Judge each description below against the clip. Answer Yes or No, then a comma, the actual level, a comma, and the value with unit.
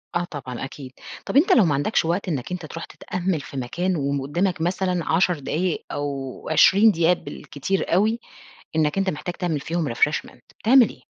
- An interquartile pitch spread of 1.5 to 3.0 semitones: No, average, 4.3 semitones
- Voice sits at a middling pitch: Yes, medium, 170 Hz